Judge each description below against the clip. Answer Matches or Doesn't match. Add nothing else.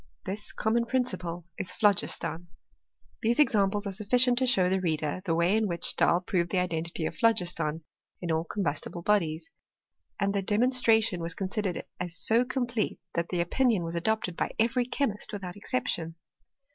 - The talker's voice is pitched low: Doesn't match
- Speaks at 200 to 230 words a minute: Doesn't match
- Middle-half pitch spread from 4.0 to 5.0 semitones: Matches